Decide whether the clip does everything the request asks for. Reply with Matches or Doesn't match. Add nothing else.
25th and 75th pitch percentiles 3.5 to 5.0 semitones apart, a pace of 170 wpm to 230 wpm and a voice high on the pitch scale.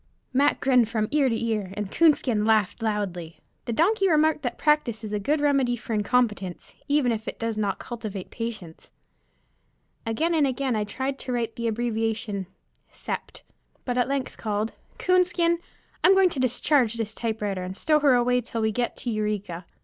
Matches